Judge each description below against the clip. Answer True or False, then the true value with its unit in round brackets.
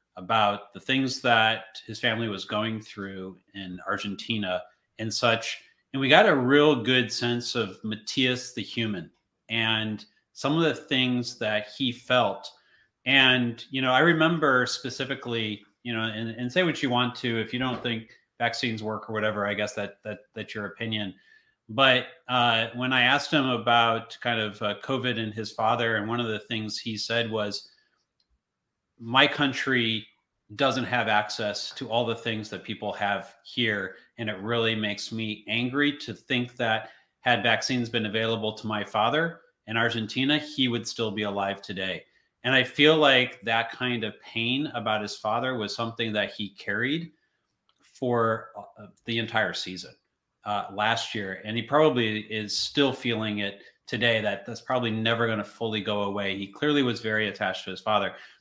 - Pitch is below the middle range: True (115 Hz)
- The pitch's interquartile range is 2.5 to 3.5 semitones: True (2.8 semitones)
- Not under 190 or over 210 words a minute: False (175 wpm)